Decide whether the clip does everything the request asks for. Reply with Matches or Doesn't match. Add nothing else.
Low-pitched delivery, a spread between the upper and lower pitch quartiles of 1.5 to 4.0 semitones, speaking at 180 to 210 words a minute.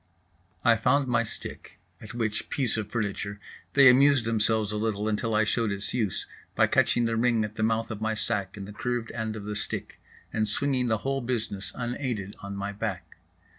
Matches